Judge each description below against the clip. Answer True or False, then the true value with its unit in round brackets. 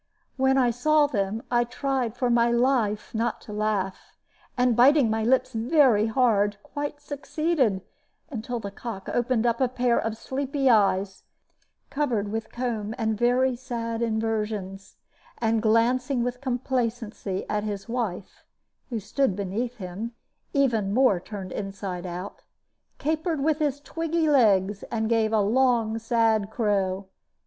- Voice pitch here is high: True (230 Hz)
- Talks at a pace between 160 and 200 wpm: False (140 wpm)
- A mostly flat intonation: False (3.5 semitones)